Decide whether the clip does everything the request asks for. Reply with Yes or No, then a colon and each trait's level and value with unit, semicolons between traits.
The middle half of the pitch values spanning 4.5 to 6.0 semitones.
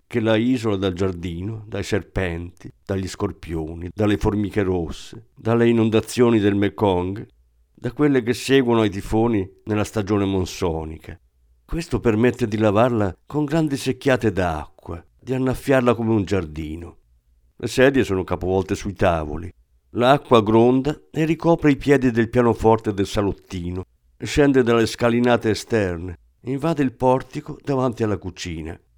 Yes: average, 5.3 semitones